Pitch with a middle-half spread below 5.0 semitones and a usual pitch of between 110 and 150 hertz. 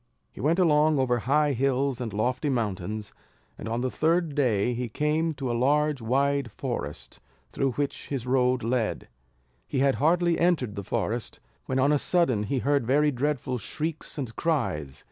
Yes: average, 4.0 semitones; low, 135 Hz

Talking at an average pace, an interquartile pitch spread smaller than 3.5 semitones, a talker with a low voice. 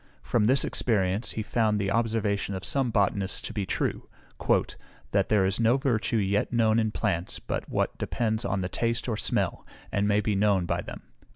Yes: average, 190 wpm; narrow, 2.5 semitones; low, 105 Hz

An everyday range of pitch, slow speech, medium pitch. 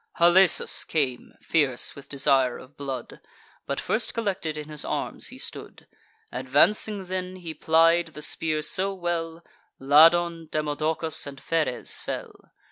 Yes: average, 3.2 semitones; slow, 130 wpm; medium, 160 Hz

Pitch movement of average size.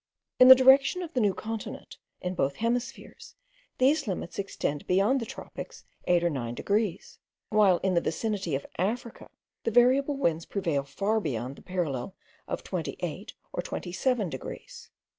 No: wide, 6.2 semitones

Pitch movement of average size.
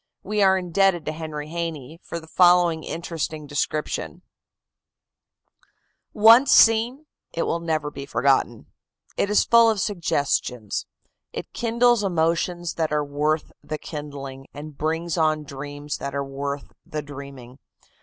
Yes: average, 3.5 semitones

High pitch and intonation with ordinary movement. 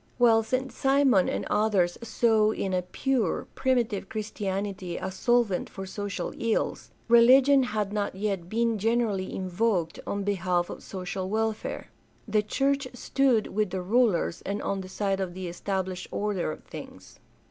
Yes: high, 205 Hz; average, 3.6 semitones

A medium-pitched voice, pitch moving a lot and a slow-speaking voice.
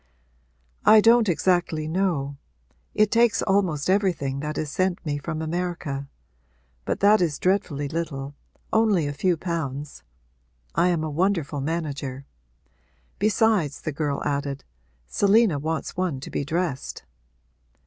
No: medium, 160 Hz; average, 4.7 semitones; slow, 130 wpm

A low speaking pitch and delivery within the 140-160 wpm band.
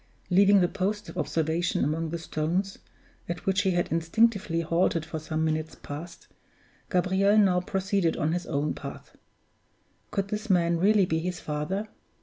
No: medium, 175 Hz; average, 155 wpm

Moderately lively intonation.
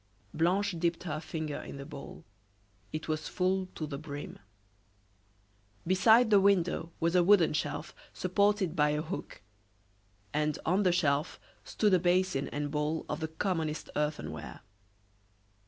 Yes: average, 3.6 semitones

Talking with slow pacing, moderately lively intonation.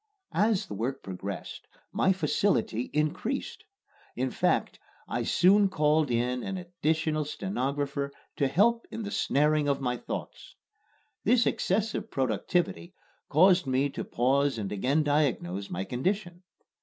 No: slow, 130 wpm; wide, 6.4 semitones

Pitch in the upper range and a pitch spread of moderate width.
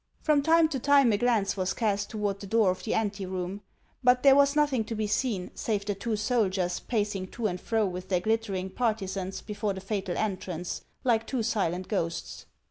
Yes: high, 210 Hz; average, 3.6 semitones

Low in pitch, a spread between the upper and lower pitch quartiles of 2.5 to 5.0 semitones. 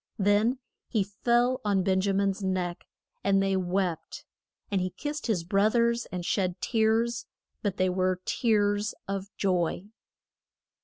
No: high, 200 Hz; average, 2.9 semitones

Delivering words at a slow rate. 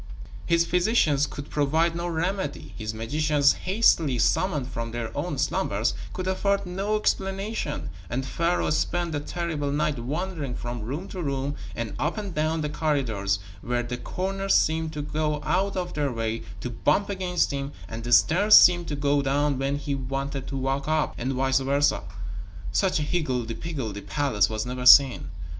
No: average, 170 wpm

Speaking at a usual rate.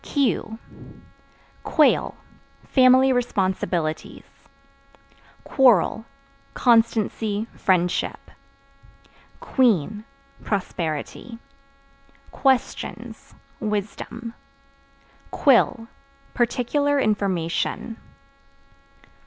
No: slow, 45 wpm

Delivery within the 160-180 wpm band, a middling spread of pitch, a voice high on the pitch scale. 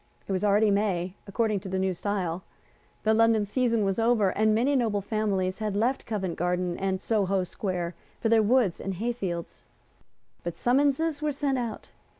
Yes: average, 170 wpm; average, 3.5 semitones; high, 210 Hz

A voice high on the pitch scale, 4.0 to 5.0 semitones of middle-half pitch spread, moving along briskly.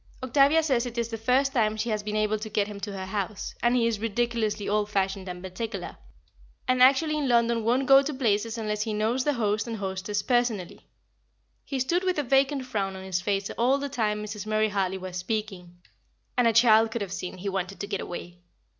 No: high, 215 Hz; average, 3.6 semitones; fast, 220 wpm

